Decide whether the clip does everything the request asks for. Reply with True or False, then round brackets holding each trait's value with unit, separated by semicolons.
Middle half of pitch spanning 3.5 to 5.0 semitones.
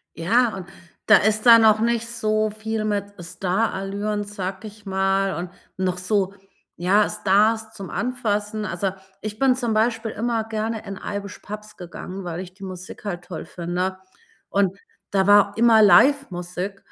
False (2.5 semitones)